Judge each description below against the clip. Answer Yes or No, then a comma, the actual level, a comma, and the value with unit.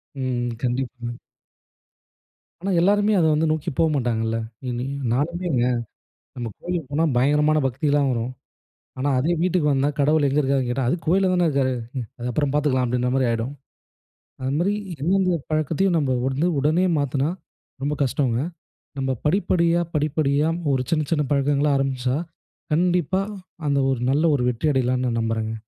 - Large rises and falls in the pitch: No, average, 3.7 semitones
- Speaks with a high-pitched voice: No, medium, 140 Hz